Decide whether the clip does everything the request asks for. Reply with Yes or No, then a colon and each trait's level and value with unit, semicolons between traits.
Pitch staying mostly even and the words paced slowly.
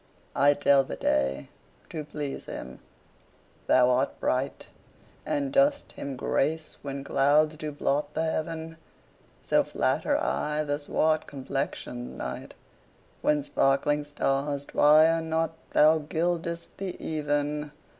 Yes: narrow, 2.3 semitones; slow, 120 wpm